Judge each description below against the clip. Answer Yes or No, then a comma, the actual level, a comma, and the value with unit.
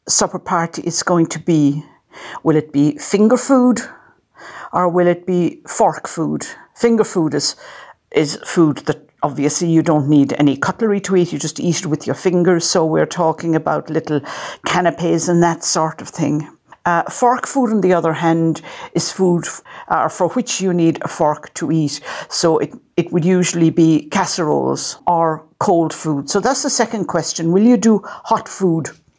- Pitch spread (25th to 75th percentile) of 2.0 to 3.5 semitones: Yes, average, 2.9 semitones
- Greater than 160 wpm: Yes, average, 180 wpm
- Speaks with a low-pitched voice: No, medium, 170 Hz